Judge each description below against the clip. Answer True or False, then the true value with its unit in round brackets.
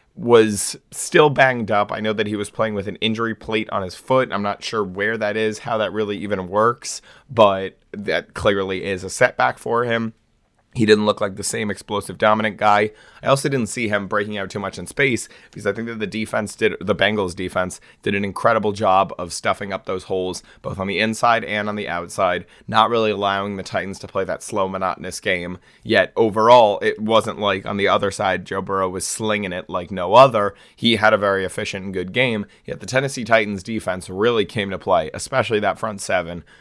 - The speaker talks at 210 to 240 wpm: True (215 wpm)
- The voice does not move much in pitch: True (2.3 semitones)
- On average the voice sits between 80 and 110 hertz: True (105 Hz)